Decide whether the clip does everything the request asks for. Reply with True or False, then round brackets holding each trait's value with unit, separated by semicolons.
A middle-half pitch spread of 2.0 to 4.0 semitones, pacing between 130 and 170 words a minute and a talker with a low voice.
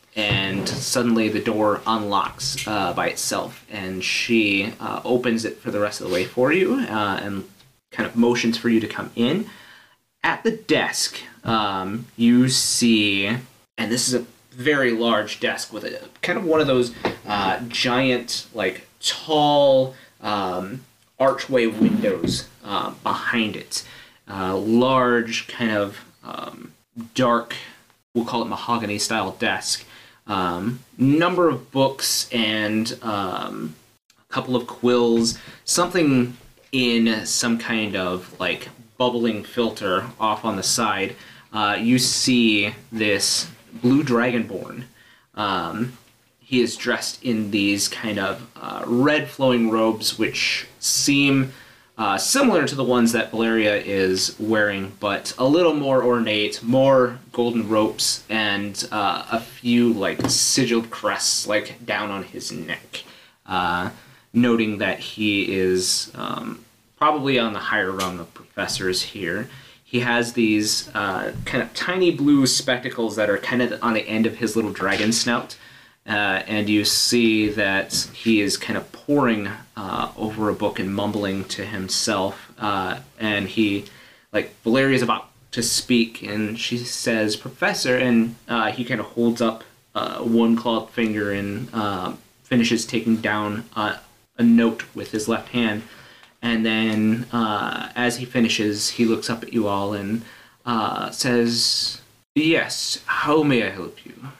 True (2.6 semitones; 145 wpm; 115 Hz)